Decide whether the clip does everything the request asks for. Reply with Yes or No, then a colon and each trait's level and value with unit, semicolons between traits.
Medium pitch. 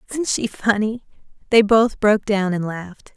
No: high, 210 Hz